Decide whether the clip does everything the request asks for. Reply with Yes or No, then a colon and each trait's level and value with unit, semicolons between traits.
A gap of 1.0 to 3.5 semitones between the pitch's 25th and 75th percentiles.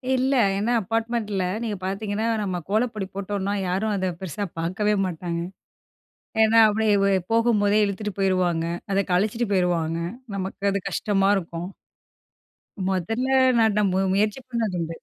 Yes: average, 2.8 semitones